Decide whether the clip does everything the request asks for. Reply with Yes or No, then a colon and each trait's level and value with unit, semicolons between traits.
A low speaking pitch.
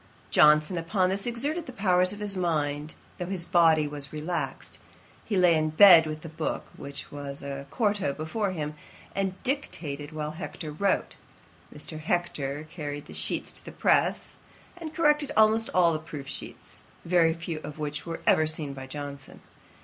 No: medium, 160 Hz